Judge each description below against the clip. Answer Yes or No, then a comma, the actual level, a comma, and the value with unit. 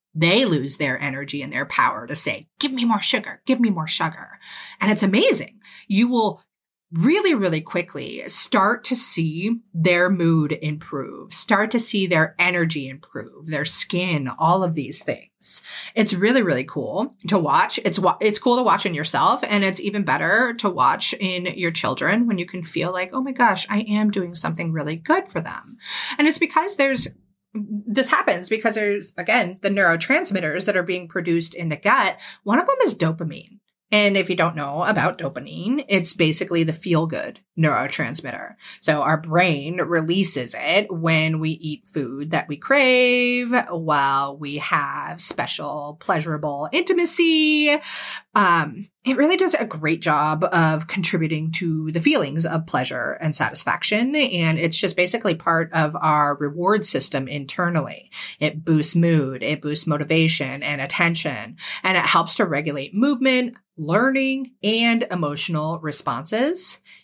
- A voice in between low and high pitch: Yes, medium, 175 Hz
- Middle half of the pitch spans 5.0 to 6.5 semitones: Yes, wide, 5.6 semitones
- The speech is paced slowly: No, average, 160 wpm